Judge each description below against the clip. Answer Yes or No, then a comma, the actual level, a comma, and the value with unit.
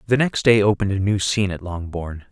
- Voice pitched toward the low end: Yes, low, 100 Hz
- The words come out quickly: Yes, fast, 235 wpm